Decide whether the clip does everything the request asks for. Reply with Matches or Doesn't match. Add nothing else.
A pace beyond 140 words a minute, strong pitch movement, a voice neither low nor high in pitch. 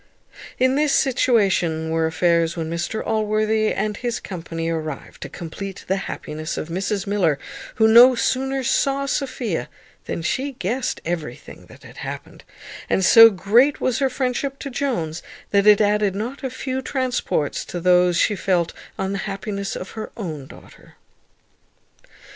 Doesn't match